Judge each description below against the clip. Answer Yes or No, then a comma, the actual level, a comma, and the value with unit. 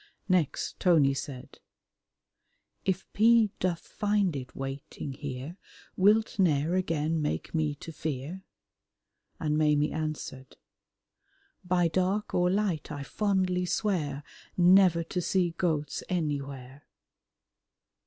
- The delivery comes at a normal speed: No, slow, 105 wpm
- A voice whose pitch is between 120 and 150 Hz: No, medium, 165 Hz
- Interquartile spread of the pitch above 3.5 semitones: Yes, average, 4.2 semitones